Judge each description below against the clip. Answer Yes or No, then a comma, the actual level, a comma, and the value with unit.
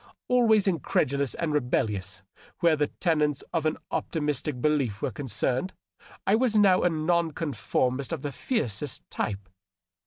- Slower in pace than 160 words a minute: Yes, average, 145 wpm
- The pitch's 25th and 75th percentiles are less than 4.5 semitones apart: No, average, 5.0 semitones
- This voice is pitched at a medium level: Yes, medium, 150 Hz